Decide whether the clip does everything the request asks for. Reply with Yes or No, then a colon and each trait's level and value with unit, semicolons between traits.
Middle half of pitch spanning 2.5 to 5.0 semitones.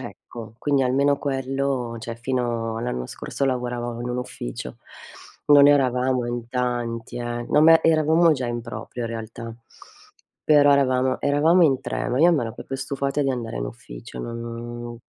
Yes: average, 2.9 semitones